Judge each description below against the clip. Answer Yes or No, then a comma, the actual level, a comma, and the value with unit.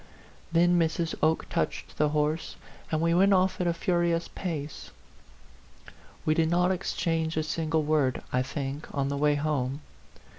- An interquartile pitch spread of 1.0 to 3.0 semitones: Yes, narrow, 2.4 semitones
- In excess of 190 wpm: No, average, 155 wpm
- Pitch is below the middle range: No, medium, 160 Hz